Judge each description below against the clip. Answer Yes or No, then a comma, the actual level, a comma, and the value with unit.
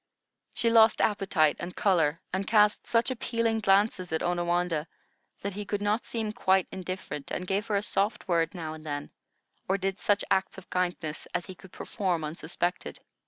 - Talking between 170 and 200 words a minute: Yes, average, 175 wpm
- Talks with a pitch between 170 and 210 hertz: Yes, high, 190 Hz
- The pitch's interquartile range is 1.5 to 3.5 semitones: Yes, average, 3.2 semitones